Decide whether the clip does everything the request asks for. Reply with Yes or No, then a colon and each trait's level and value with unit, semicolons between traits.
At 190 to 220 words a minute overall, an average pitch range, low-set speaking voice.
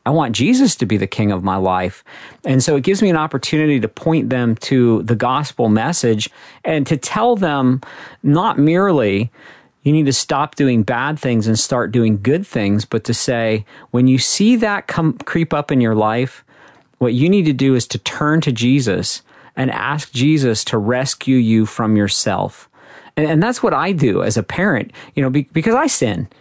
Yes: average, 200 wpm; average, 5.0 semitones; low, 130 Hz